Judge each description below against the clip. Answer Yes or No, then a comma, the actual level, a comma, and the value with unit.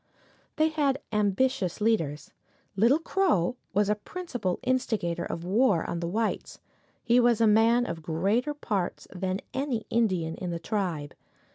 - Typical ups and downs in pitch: No, wide, 5.9 semitones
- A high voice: Yes, high, 210 Hz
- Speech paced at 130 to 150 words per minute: Yes, average, 145 wpm